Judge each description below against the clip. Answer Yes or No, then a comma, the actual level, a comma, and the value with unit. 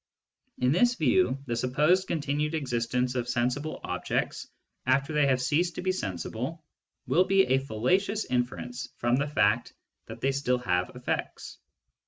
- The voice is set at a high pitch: No, low, 135 Hz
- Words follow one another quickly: No, average, 150 wpm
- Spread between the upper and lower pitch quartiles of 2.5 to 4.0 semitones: No, average, 4.4 semitones